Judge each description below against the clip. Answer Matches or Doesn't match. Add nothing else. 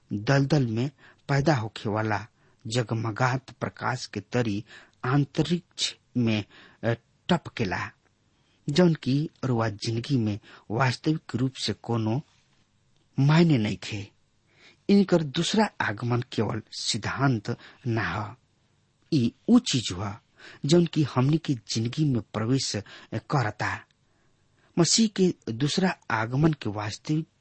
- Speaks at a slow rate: Matches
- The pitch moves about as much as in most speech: Matches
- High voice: Doesn't match